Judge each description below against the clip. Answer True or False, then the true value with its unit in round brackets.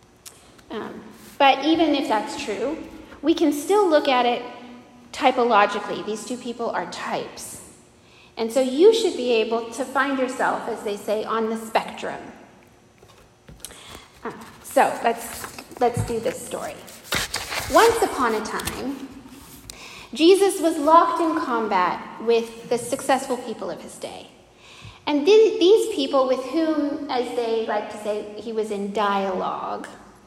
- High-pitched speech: True (250 Hz)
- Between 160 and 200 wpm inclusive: False (140 wpm)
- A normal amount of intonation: True (4.8 semitones)